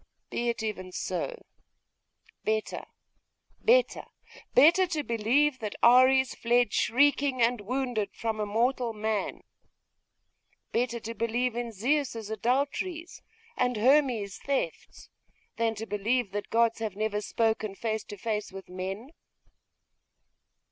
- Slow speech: Yes, slow, 120 wpm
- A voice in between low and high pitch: No, high, 230 Hz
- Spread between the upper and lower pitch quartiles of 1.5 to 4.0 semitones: Yes, average, 3.3 semitones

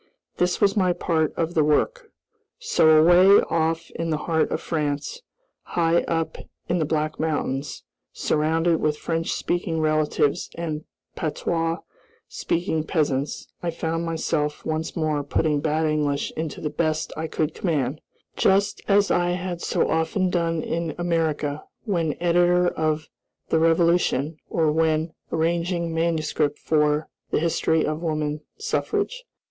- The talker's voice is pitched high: No, medium, 160 Hz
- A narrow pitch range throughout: Yes, narrow, 1.9 semitones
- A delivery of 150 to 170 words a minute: No, average, 140 wpm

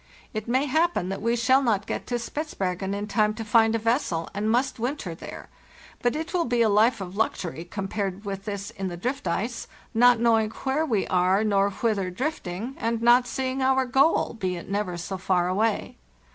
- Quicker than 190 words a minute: Yes, average, 200 wpm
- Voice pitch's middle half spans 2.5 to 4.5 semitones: Yes, average, 4.1 semitones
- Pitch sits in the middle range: No, high, 220 Hz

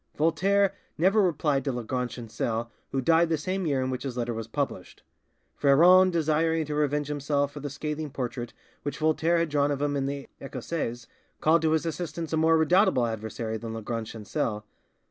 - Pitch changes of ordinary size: Yes, average, 4.8 semitones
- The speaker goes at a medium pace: Yes, average, 185 wpm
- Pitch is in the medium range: Yes, medium, 145 Hz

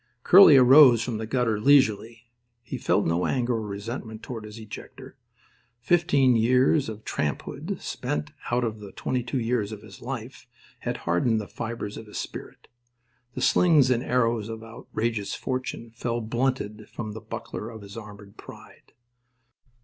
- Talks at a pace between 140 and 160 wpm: Yes, average, 155 wpm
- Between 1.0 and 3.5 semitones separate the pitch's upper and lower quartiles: Yes, average, 2.9 semitones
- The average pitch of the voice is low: Yes, low, 115 Hz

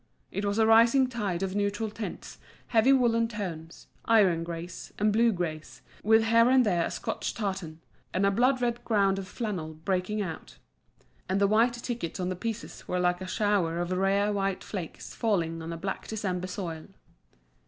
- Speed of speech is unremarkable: Yes, average, 180 wpm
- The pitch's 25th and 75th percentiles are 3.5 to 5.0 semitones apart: Yes, average, 3.9 semitones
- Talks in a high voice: Yes, high, 200 Hz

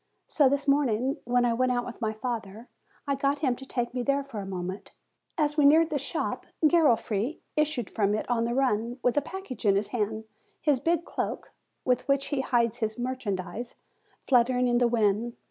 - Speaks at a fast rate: No, average, 195 wpm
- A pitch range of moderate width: Yes, average, 3.8 semitones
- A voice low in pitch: No, high, 245 Hz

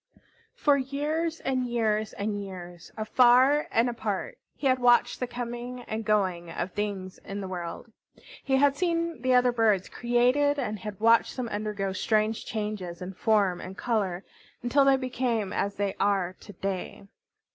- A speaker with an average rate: Yes, average, 160 wpm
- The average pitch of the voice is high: Yes, high, 220 Hz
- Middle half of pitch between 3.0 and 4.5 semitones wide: Yes, average, 4.2 semitones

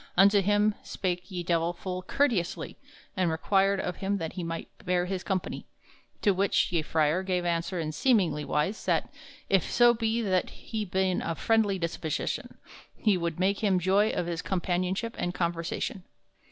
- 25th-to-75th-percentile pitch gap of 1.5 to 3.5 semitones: Yes, average, 2.7 semitones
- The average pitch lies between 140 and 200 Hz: Yes, medium, 185 Hz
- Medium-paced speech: Yes, average, 165 wpm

